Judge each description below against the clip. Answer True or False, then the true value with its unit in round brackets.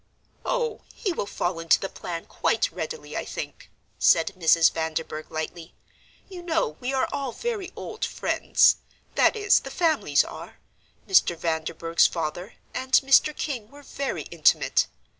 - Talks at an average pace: True (145 wpm)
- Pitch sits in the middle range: False (245 Hz)